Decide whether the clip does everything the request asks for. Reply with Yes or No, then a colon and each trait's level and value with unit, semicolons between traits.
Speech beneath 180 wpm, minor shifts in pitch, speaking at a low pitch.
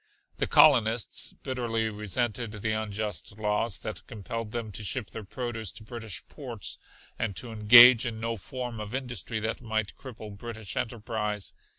Yes: average, 155 wpm; narrow, 1.9 semitones; low, 110 Hz